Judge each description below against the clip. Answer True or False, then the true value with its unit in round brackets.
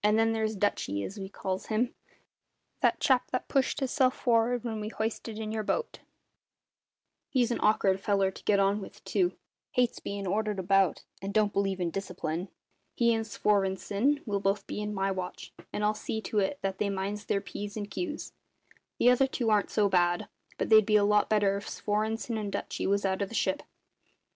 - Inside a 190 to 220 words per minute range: True (195 wpm)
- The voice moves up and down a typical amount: False (2.3 semitones)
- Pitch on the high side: True (210 Hz)